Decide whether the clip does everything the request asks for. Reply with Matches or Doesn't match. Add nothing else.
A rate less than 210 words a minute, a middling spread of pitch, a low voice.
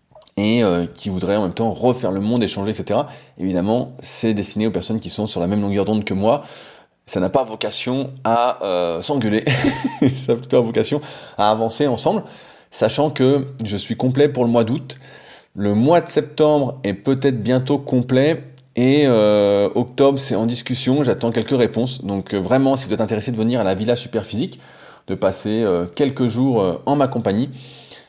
Matches